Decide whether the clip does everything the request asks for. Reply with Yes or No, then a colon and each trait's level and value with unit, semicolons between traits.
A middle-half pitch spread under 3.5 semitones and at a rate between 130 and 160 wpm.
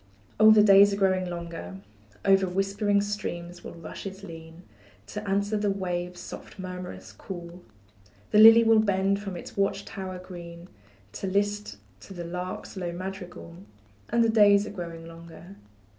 Yes: narrow, 2.5 semitones; average, 155 wpm